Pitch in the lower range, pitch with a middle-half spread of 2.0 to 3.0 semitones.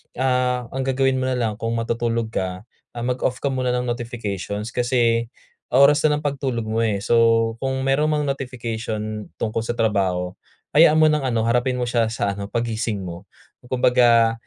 Yes: low, 120 Hz; narrow, 2.5 semitones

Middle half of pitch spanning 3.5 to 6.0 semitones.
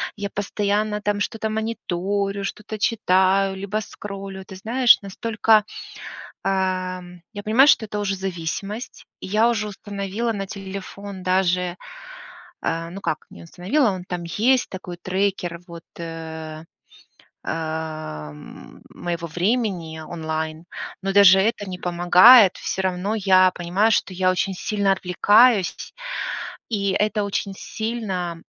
No: average, 2.8 semitones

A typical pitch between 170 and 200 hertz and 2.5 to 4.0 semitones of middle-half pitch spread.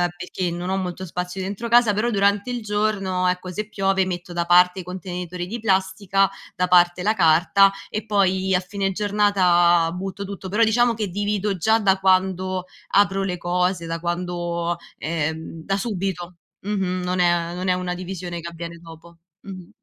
No: medium, 185 Hz; narrow, 2.1 semitones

